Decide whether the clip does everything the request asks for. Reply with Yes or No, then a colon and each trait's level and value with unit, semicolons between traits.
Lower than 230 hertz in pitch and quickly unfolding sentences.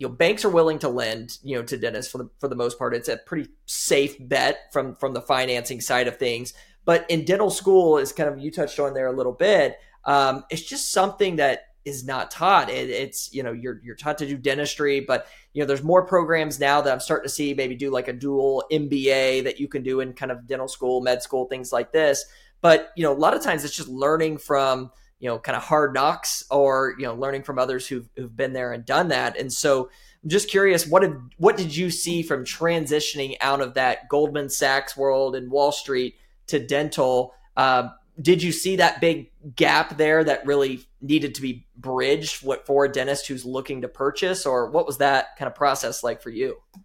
Yes: medium, 140 Hz; fast, 230 wpm